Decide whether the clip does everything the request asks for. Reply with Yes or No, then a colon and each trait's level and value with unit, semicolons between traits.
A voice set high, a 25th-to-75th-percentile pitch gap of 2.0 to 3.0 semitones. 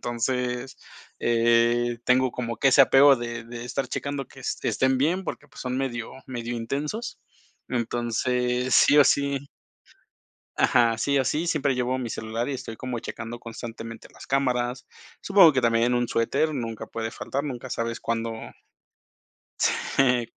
No: low, 125 Hz; narrow, 2.4 semitones